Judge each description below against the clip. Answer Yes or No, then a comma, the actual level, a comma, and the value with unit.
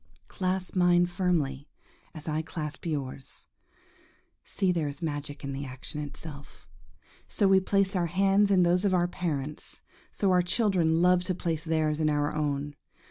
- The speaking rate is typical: Yes, average, 160 wpm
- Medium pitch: Yes, medium, 165 Hz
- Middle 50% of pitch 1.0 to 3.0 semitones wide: No, average, 3.7 semitones